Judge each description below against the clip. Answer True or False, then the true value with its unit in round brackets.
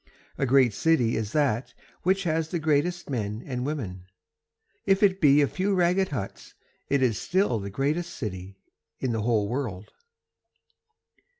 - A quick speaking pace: False (155 wpm)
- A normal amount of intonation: False (7.0 semitones)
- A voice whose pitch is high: False (135 Hz)